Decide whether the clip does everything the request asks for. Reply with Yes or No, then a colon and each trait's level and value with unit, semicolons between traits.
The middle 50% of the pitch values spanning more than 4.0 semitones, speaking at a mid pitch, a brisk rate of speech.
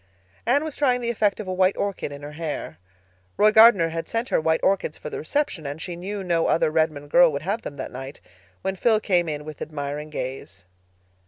Yes: wide, 5.6 semitones; medium, 165 Hz; fast, 215 wpm